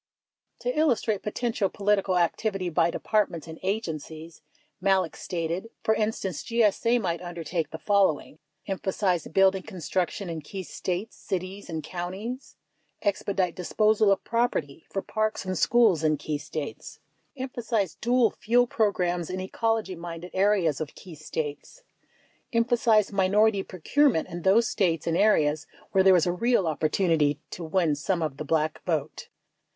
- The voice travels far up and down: No, average, 4.5 semitones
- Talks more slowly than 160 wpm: Yes, average, 150 wpm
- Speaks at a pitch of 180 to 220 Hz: Yes, medium, 185 Hz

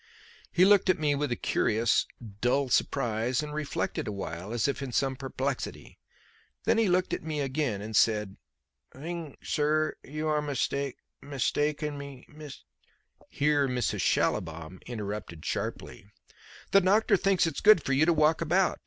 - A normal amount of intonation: Yes, average, 4.4 semitones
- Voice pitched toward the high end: No, medium, 140 Hz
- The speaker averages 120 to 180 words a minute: Yes, average, 155 wpm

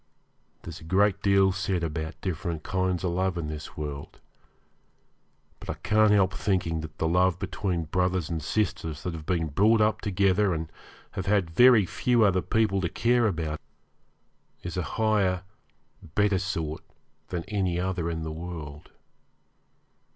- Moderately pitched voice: No, very low, 90 Hz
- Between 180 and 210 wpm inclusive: No, average, 155 wpm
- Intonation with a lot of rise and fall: No, average, 3.3 semitones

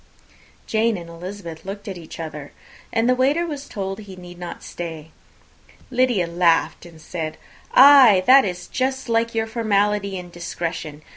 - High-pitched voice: Yes, high, 195 Hz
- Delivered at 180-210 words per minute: No, average, 160 wpm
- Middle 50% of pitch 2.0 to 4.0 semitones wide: No, average, 5.2 semitones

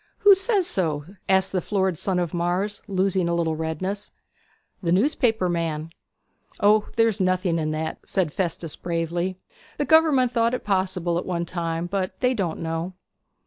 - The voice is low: No, medium, 185 Hz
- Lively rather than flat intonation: No, average, 3.5 semitones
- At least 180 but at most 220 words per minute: No, average, 160 wpm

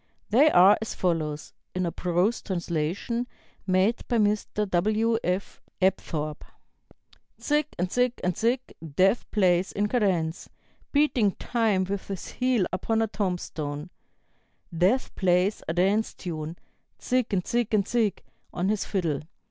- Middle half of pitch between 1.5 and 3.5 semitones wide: No, average, 4.1 semitones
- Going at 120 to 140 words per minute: Yes, slow, 135 wpm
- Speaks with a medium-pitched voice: No, high, 195 Hz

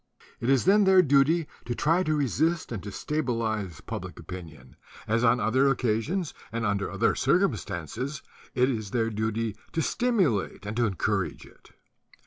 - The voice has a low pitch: Yes, low, 120 Hz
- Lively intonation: Yes, wide, 6.1 semitones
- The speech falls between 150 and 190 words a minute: Yes, average, 155 wpm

